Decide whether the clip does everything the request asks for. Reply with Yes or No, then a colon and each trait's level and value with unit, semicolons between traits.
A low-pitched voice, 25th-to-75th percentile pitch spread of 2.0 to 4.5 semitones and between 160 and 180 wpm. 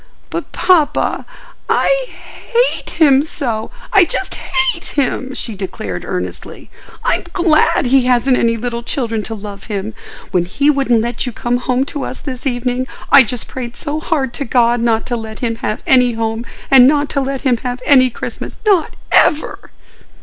No: very high, 250 Hz; average, 3.7 semitones; average, 165 wpm